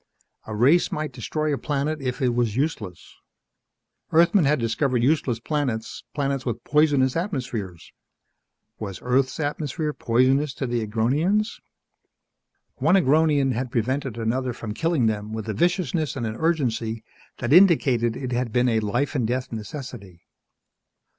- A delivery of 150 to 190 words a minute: No, average, 140 wpm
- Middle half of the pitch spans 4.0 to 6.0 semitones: Yes, average, 4.6 semitones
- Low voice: Yes, low, 130 Hz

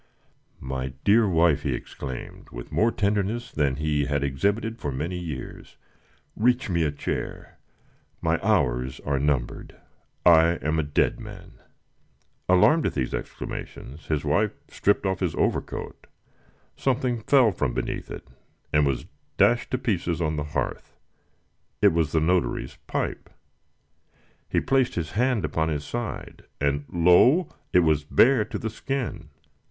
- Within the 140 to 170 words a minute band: Yes, average, 145 wpm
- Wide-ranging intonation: Yes, wide, 6.8 semitones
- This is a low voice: Yes, very low, 85 Hz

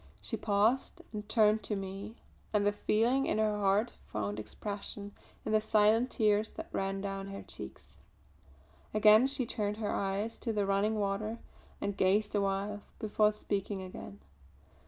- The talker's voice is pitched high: Yes, high, 210 Hz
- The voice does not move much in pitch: Yes, narrow, 1.6 semitones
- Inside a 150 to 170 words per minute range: Yes, average, 155 wpm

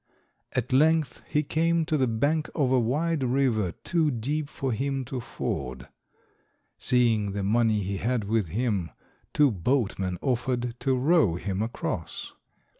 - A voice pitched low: Yes, low, 125 Hz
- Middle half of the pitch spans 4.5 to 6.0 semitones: Yes, average, 4.9 semitones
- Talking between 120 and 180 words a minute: Yes, average, 145 wpm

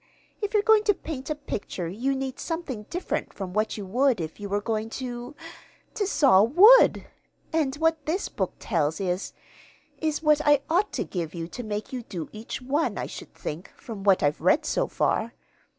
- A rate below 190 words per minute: No, average, 195 wpm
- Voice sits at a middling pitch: No, very high, 250 Hz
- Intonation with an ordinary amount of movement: No, wide, 7.6 semitones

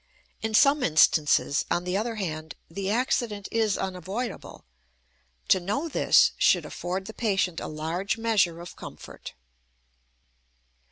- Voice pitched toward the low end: No, high, 195 Hz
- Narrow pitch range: No, average, 4.3 semitones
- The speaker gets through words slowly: Yes, slow, 125 wpm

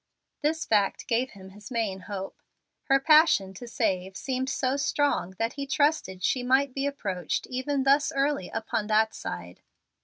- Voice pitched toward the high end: Yes, high, 245 Hz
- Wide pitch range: Yes, wide, 6.1 semitones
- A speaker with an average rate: Yes, average, 160 wpm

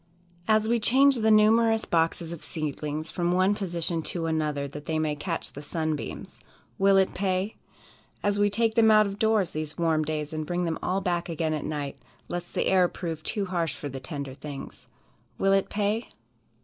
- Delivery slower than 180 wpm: No, average, 190 wpm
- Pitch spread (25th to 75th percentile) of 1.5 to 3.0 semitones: No, average, 4.7 semitones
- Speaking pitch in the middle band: Yes, medium, 175 Hz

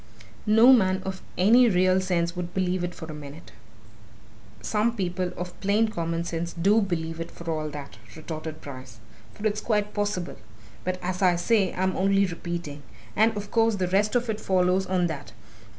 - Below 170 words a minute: No, average, 180 wpm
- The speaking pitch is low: No, medium, 185 Hz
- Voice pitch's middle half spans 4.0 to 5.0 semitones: No, average, 3.4 semitones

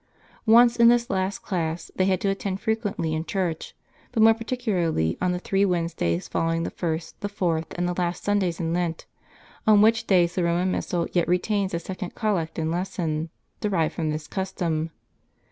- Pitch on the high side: No, medium, 180 Hz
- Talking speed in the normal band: Yes, average, 185 wpm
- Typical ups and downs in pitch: Yes, average, 3.4 semitones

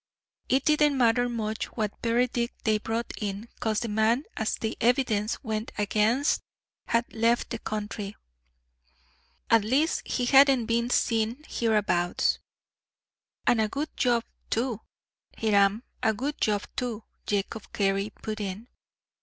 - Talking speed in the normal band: No, slow, 130 wpm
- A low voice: No, high, 225 Hz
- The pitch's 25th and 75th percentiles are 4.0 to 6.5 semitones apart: No, narrow, 2.4 semitones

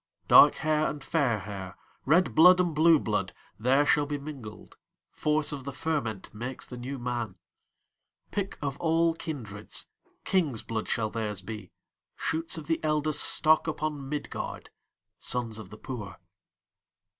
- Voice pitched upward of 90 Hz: Yes, medium, 140 Hz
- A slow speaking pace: Yes, slow, 115 wpm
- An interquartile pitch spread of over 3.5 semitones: Yes, wide, 5.5 semitones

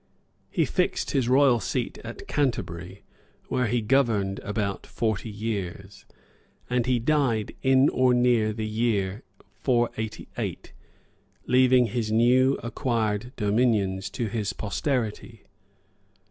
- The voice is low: Yes, low, 115 Hz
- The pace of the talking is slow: Yes, slow, 110 wpm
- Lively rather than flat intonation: No, average, 3.3 semitones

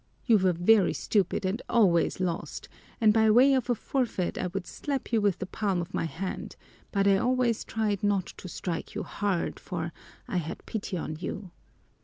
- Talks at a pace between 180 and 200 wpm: Yes, average, 190 wpm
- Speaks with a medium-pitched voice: No, high, 200 Hz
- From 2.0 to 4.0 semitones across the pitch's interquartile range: Yes, average, 3.7 semitones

